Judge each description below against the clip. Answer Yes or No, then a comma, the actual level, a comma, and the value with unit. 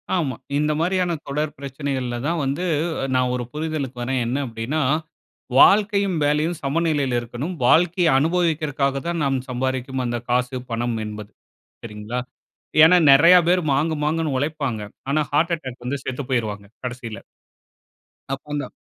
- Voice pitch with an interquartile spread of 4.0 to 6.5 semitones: Yes, average, 4.3 semitones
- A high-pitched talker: No, medium, 140 Hz